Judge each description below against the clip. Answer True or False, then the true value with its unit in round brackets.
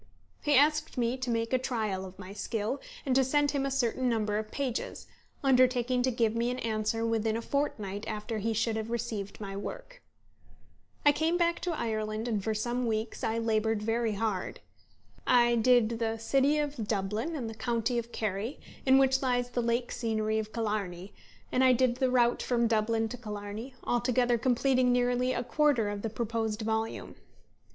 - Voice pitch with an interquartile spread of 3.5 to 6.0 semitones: False (2.7 semitones)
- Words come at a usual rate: True (185 wpm)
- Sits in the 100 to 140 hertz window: False (230 Hz)